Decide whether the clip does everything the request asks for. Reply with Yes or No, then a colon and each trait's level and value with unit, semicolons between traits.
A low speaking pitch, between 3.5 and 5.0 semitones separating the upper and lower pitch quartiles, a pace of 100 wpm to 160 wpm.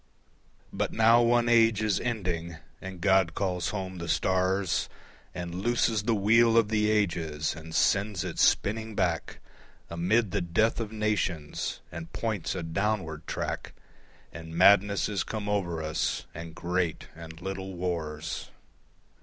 Yes: very low, 95 Hz; average, 4.2 semitones; average, 140 wpm